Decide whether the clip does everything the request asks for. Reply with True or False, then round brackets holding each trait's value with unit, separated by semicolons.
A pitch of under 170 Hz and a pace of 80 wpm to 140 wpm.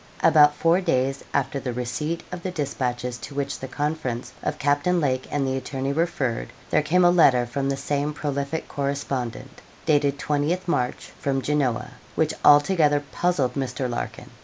False (140 Hz; 160 wpm)